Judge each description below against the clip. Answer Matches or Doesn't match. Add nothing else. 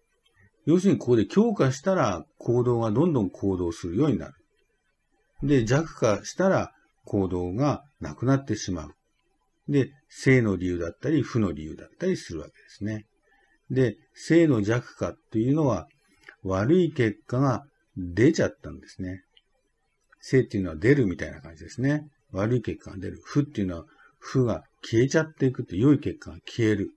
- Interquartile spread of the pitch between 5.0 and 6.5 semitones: Doesn't match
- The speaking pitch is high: Doesn't match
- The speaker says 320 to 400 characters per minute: Matches